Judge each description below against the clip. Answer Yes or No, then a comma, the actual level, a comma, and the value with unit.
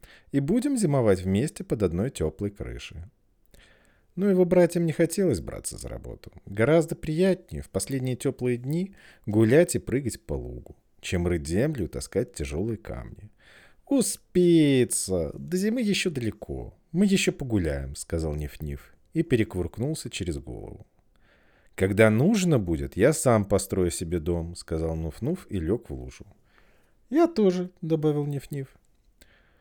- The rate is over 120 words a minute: Yes, average, 140 wpm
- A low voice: Yes, low, 120 Hz